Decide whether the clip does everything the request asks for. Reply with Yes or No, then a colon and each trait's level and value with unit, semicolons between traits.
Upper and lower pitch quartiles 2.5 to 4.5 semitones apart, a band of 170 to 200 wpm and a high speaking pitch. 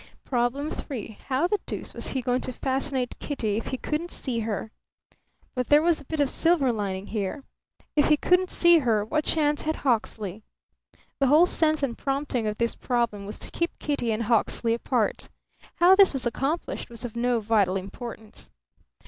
No: average, 4.9 semitones; average, 180 wpm; very high, 250 Hz